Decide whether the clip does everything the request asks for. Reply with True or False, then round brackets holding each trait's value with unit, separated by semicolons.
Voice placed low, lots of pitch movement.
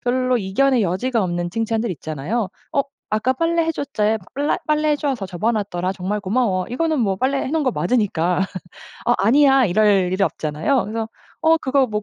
False (225 Hz; 5.9 semitones)